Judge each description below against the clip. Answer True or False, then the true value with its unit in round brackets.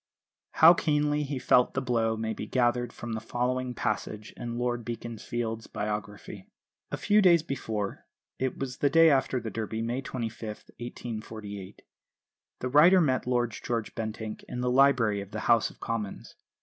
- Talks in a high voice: False (120 Hz)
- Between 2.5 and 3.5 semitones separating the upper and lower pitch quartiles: True (2.9 semitones)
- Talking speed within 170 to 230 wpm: False (160 wpm)